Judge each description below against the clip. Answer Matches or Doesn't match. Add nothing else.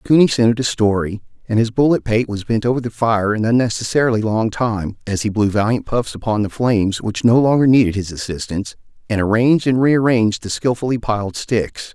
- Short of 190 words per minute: Doesn't match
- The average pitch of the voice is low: Matches